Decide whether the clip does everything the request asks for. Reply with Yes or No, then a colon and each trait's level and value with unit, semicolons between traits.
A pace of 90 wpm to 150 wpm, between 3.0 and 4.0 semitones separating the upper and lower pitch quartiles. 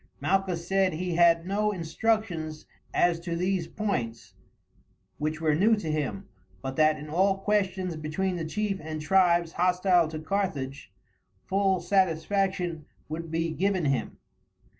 Yes: average, 140 wpm; average, 3.5 semitones